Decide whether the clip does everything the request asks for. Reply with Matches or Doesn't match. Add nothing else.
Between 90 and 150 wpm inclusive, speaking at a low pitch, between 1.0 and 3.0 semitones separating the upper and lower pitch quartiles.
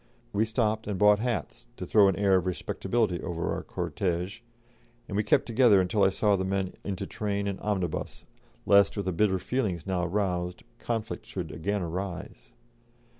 Doesn't match